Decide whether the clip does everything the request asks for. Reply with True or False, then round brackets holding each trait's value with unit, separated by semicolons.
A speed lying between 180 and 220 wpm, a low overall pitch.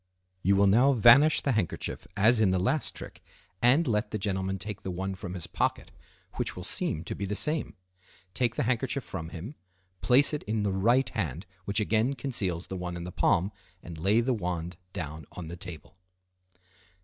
True (195 wpm; 100 Hz)